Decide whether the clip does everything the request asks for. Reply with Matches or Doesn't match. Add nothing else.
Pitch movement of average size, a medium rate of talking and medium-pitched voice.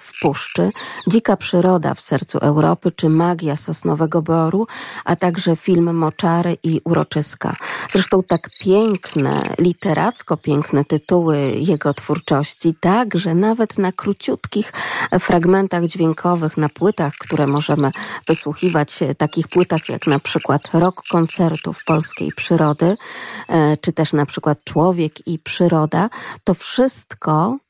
Matches